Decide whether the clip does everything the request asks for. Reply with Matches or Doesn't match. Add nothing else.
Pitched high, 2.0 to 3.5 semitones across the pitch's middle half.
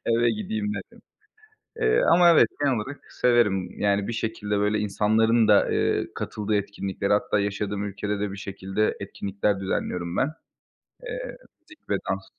Doesn't match